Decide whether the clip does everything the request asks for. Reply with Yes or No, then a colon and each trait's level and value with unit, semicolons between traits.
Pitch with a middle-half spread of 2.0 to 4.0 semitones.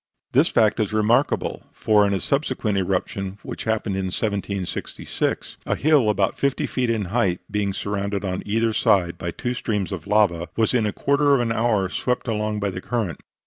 Yes: average, 2.9 semitones